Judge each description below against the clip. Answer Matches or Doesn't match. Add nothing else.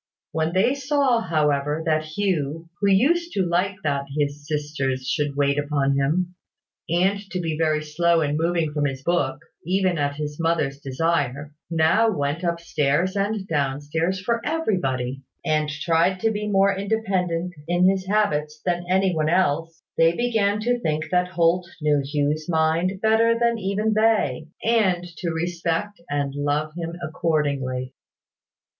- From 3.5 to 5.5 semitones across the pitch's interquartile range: Matches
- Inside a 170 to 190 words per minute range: Doesn't match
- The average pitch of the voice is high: Doesn't match